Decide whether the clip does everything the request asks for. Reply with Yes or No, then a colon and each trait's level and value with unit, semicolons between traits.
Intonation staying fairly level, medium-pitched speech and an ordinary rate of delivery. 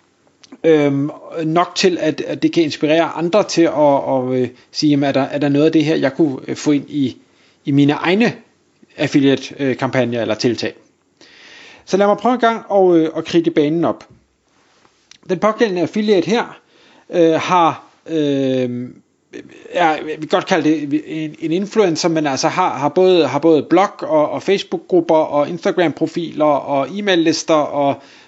No: average, 3.4 semitones; medium, 155 Hz; average, 165 wpm